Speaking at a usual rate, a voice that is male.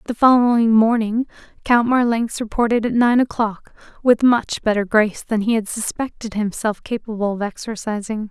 No: average, 150 wpm; female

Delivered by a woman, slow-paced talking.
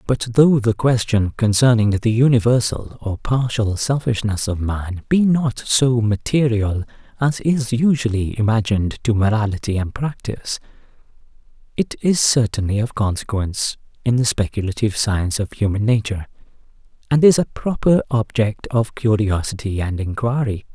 No: male; slow, 130 wpm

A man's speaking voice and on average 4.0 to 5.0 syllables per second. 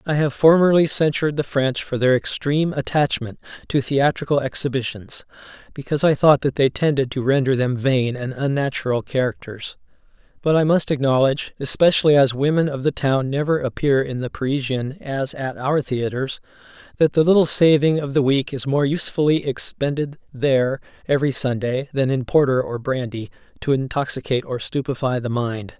No: male; 5.4 syllables/s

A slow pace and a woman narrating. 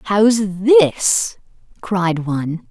Yes: slow, 90 wpm; female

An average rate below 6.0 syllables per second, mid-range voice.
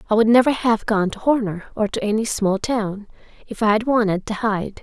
No: 5.3 syllables/s; high, 220 Hz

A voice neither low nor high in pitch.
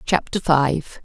Yes: medium, 160 Hz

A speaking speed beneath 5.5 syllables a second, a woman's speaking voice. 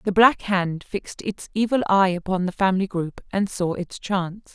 Yes: 5.0 syllables/s; female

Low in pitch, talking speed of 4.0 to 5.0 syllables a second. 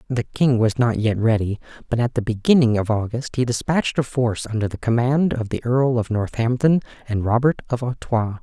No: low, 120 Hz; 5.4 syllables/s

